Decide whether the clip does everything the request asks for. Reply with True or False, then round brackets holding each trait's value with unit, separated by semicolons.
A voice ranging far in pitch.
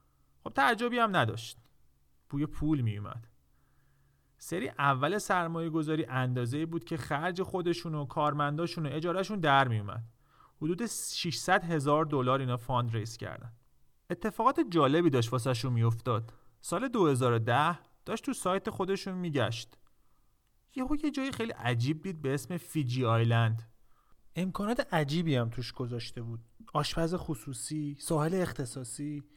True (6.3 semitones)